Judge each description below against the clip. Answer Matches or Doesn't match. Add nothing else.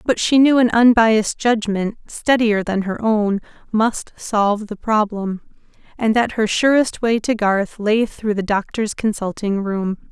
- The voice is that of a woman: Matches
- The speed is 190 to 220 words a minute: Doesn't match